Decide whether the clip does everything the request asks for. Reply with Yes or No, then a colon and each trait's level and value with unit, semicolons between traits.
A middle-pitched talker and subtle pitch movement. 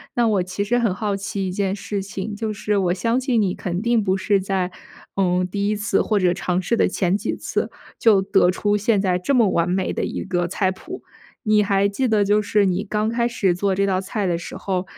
No: high, 200 Hz; narrow, 2.2 semitones